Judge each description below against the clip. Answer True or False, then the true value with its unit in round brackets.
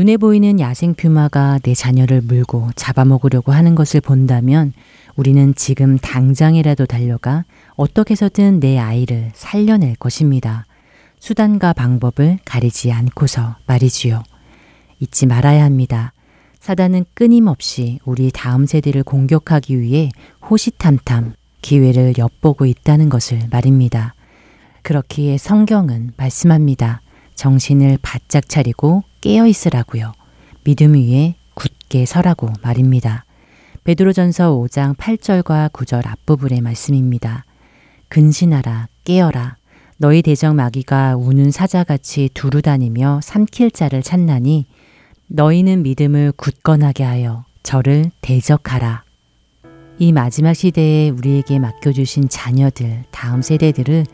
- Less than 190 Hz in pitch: True (140 Hz)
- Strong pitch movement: False (3.9 semitones)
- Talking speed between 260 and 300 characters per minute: True (280 characters per minute)